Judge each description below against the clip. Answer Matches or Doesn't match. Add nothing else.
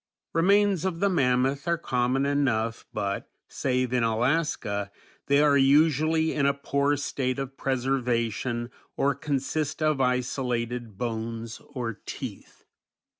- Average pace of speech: Doesn't match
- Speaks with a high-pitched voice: Doesn't match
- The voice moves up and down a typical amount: Matches